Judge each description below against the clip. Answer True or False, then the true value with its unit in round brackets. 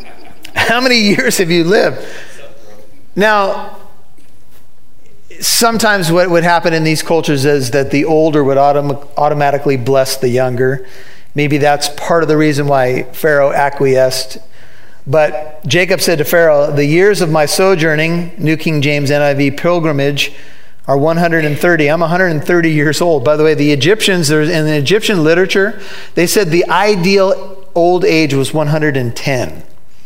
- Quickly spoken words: False (140 wpm)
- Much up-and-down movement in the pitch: False (3.7 semitones)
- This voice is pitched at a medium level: True (155 Hz)